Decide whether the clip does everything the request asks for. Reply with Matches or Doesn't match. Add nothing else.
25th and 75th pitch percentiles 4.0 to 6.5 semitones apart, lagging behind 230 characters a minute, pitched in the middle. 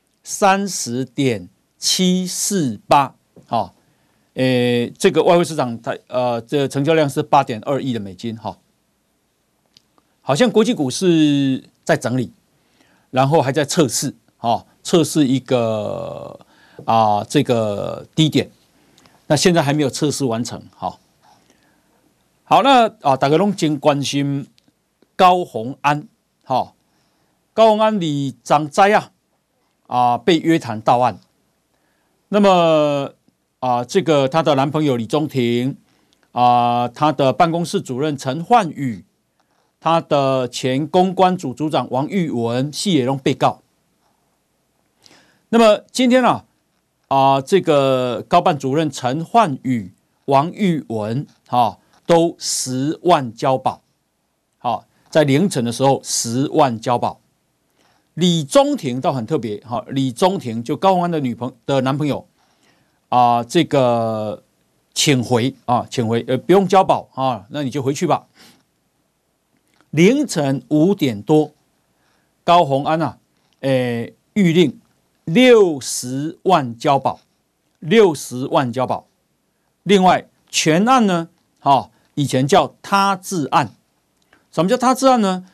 Matches